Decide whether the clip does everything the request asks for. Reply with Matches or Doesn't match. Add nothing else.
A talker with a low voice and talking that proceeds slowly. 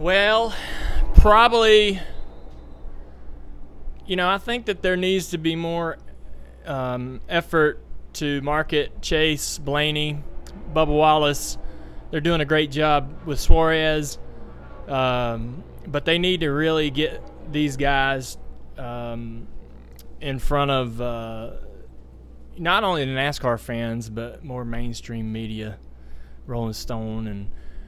Matches